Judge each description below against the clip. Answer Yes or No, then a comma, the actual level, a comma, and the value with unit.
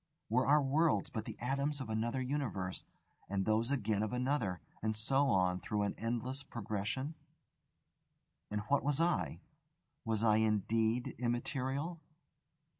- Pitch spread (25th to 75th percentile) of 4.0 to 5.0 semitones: Yes, average, 4.3 semitones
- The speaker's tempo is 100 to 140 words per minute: Yes, slow, 135 wpm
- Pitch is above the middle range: No, low, 120 Hz